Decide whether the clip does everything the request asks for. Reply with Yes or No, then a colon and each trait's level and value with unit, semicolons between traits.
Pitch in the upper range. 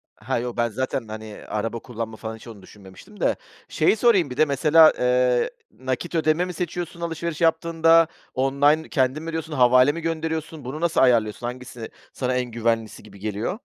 No: low, 130 Hz